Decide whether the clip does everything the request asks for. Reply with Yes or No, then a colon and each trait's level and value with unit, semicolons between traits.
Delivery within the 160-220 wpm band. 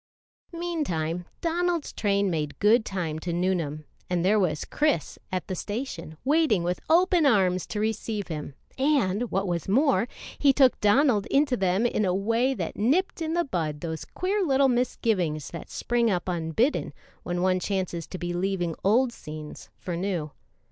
Yes: average, 165 wpm